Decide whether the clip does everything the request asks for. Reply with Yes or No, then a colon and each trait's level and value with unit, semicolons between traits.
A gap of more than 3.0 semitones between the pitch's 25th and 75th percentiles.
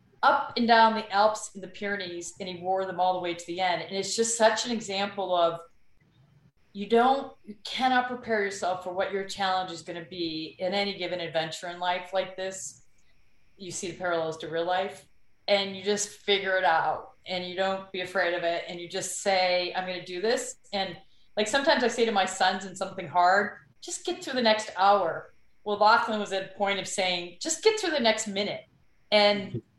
No: narrow, 2.6 semitones